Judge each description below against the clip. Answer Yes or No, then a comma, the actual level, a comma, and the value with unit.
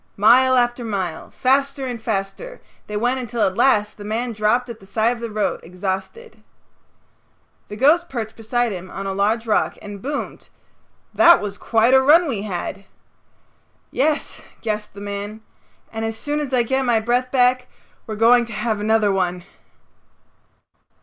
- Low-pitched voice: No, high, 225 Hz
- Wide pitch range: No, average, 3.5 semitones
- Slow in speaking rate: No, average, 165 wpm